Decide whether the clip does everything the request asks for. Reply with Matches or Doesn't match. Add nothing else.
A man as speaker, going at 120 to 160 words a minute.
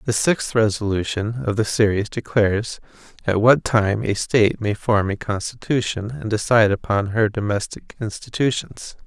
Matches